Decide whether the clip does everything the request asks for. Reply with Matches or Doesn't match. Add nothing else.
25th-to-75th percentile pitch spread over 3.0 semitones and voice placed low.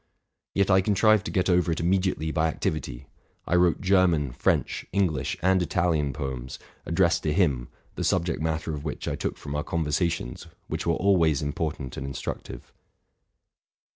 Matches